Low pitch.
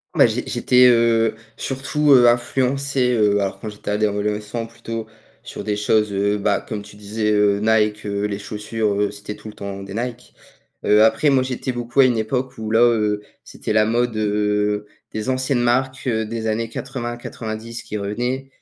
Yes: low, 110 Hz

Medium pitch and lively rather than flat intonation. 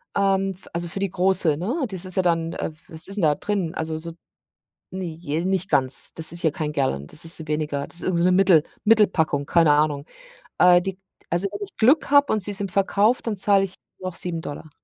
No: medium, 175 Hz; average, 3.6 semitones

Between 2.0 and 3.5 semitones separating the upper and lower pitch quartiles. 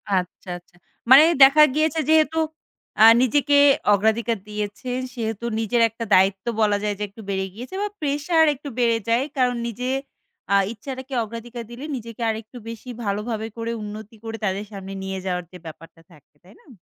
No: average, 4.0 semitones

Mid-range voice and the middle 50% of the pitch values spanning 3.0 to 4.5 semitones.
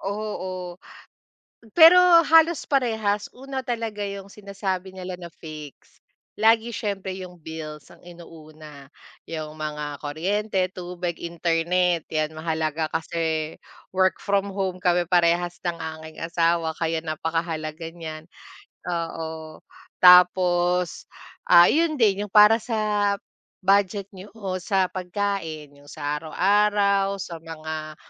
Yes: medium, 180 Hz; average, 3.8 semitones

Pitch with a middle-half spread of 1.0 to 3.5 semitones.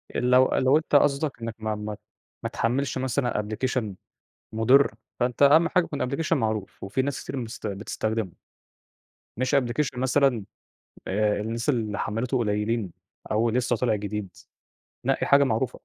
No: average, 3.9 semitones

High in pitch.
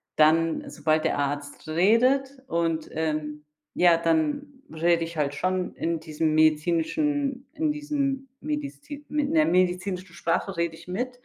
No: medium, 180 Hz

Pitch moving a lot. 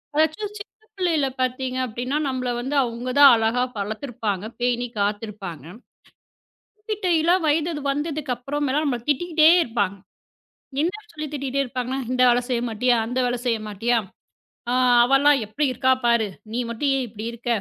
No: average, 4.0 semitones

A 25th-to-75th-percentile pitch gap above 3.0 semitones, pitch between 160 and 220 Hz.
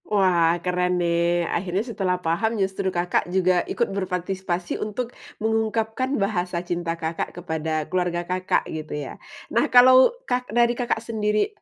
Yes: average, 4.1 semitones; medium, 185 Hz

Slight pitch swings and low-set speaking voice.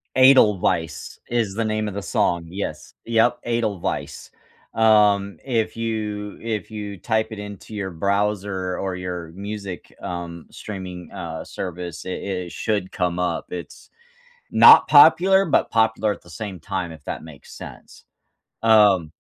No: average, 3.4 semitones; low, 100 Hz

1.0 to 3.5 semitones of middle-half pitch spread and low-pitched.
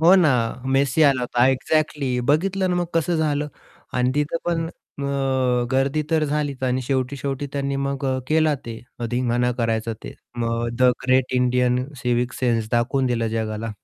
Yes: average, 3.1 semitones; low, 130 Hz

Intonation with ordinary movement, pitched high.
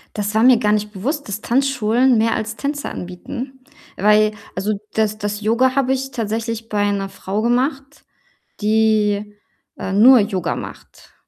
Yes: average, 3.5 semitones; high, 220 Hz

